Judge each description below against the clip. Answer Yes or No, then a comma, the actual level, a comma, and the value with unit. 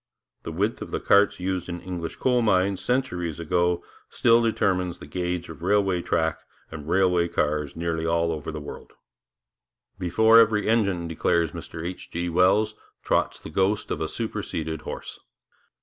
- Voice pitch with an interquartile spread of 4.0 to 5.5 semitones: No, average, 3.2 semitones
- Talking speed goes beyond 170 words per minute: No, average, 160 wpm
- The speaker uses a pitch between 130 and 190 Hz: No, very low, 90 Hz